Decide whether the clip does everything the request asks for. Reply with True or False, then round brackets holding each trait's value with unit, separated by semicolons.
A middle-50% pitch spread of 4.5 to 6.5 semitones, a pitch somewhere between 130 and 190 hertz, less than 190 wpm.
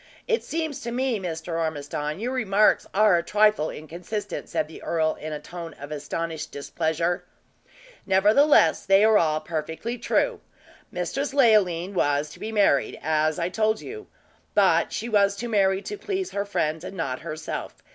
True (5.4 semitones; 185 Hz; 165 wpm)